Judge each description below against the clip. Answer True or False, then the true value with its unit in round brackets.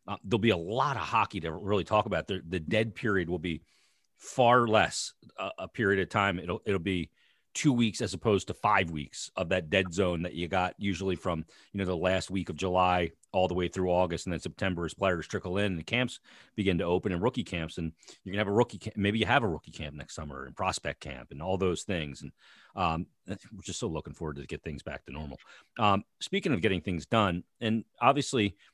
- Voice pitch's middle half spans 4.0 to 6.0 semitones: False (3.1 semitones)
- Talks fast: True (235 wpm)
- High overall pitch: False (95 Hz)